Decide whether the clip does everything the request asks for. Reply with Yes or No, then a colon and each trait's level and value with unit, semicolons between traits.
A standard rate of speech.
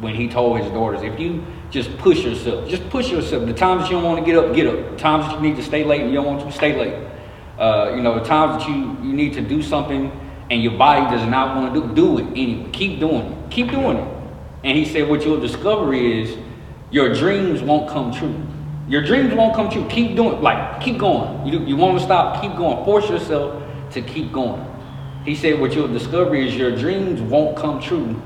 No: fast, 240 wpm